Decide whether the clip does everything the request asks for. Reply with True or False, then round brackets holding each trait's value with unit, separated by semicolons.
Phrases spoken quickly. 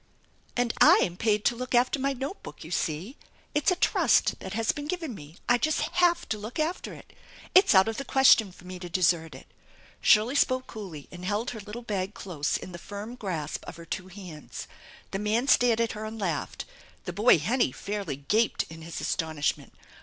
True (210 wpm)